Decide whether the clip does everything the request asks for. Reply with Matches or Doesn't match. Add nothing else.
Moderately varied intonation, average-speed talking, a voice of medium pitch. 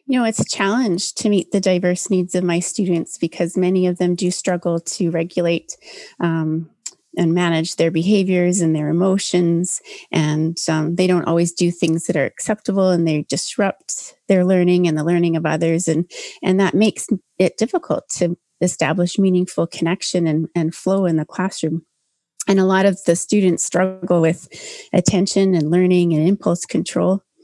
Doesn't match